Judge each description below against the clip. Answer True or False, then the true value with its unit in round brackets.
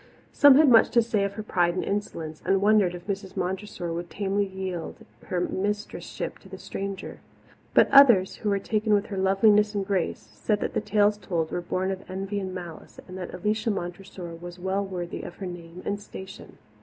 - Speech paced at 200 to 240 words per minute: True (205 wpm)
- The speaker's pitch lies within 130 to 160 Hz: False (195 Hz)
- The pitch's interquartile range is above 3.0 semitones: False (2.6 semitones)